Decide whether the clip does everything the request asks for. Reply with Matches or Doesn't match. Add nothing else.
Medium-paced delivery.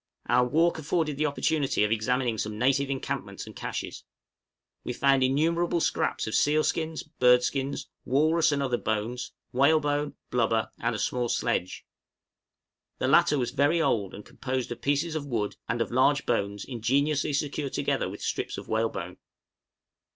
Matches